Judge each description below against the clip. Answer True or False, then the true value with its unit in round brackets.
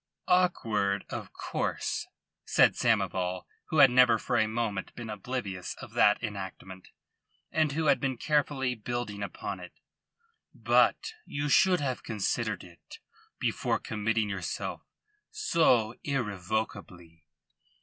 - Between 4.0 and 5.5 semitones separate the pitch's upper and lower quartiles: True (5.1 semitones)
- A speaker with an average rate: False (120 wpm)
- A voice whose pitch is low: True (110 Hz)